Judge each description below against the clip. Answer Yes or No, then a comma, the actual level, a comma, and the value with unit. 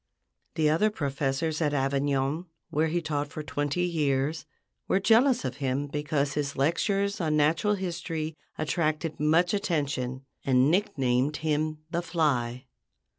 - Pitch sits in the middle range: Yes, medium, 150 Hz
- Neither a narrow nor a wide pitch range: Yes, average, 3.2 semitones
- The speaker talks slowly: Yes, slow, 130 wpm